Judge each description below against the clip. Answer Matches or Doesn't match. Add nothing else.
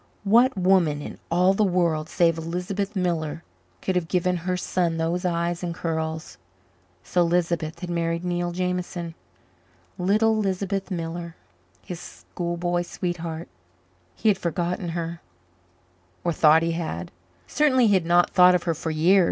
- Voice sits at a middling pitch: Matches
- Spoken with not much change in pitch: Matches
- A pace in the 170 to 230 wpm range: Doesn't match